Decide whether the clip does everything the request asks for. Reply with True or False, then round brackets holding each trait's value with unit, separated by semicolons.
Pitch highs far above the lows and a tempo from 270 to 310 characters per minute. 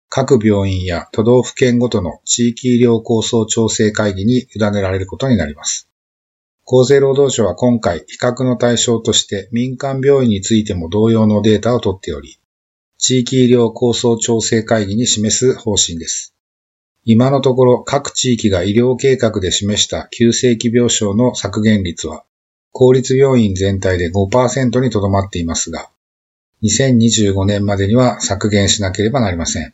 False (3.8 semitones; 300 characters per minute)